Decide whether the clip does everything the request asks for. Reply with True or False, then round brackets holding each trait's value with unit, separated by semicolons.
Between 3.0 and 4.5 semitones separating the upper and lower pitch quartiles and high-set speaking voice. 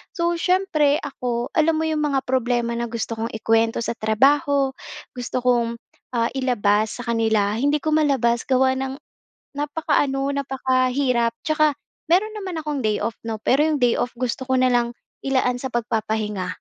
True (3.7 semitones; 255 Hz)